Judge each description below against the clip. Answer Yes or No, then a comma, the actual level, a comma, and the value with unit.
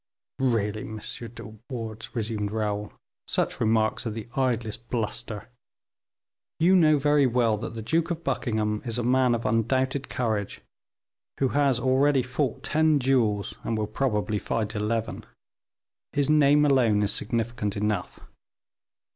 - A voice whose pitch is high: No, low, 115 Hz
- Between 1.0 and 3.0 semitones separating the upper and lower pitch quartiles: No, average, 3.6 semitones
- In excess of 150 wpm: No, average, 140 wpm